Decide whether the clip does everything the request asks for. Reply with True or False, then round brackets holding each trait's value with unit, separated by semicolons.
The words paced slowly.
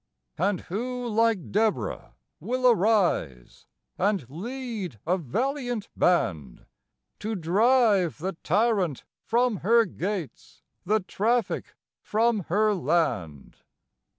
True (95 wpm)